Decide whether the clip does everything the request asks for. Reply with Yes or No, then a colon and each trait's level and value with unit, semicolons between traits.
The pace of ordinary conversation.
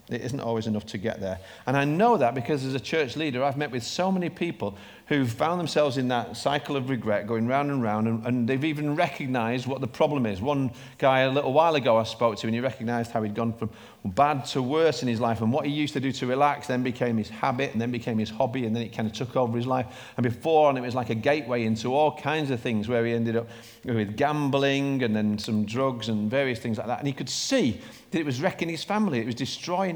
No: fast, 265 wpm